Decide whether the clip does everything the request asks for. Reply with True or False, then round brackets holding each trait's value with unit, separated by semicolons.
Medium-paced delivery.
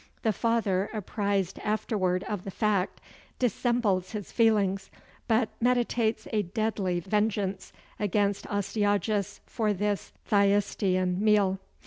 False (105 wpm)